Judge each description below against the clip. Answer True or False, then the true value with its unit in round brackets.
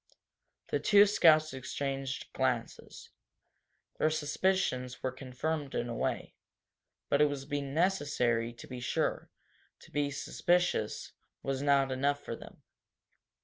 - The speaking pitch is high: False (140 Hz)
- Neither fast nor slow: False (120 wpm)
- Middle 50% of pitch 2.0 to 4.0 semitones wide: True (3.2 semitones)